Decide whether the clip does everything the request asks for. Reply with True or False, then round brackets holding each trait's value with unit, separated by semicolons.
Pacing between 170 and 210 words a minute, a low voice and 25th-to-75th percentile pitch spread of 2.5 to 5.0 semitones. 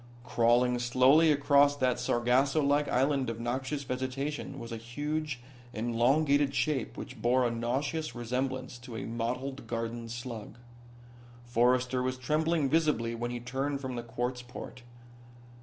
False (140 wpm; 125 Hz; 2.8 semitones)